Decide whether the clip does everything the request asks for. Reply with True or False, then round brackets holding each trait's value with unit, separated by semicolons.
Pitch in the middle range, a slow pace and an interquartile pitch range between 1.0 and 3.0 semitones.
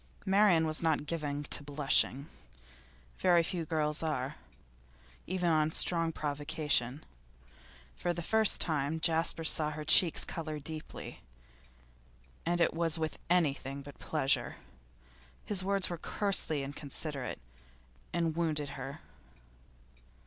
True (155 Hz; 115 wpm; 2.6 semitones)